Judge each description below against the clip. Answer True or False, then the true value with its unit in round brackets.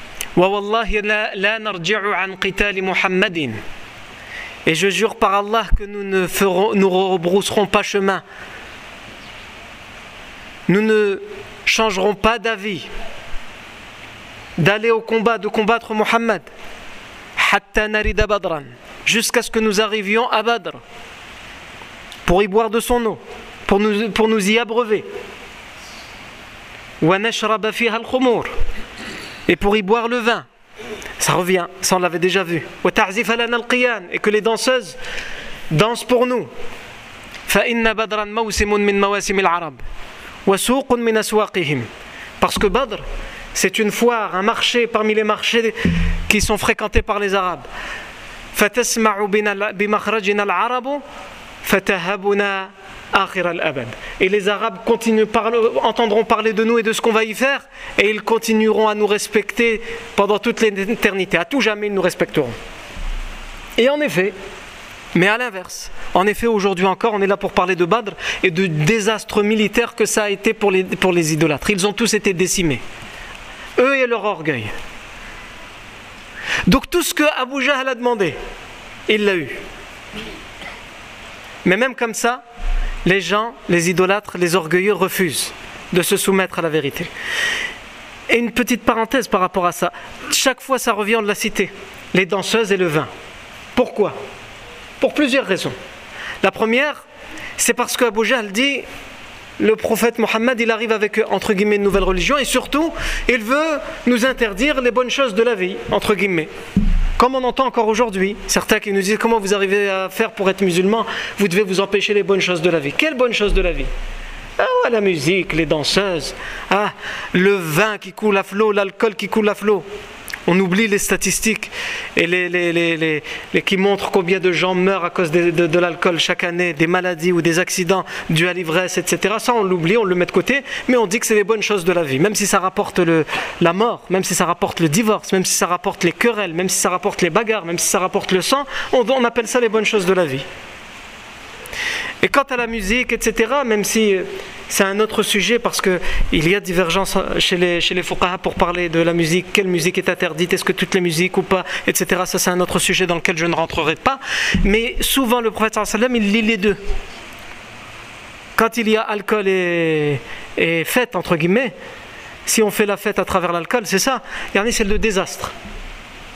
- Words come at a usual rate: True (170 wpm)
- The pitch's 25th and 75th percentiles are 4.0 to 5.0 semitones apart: False (3.5 semitones)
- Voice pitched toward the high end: True (205 Hz)